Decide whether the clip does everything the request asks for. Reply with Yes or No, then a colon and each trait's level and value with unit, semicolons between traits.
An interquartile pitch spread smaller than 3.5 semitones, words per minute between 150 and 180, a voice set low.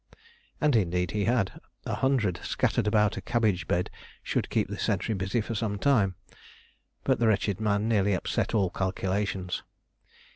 Yes: average, 2.9 semitones; average, 155 wpm; low, 105 Hz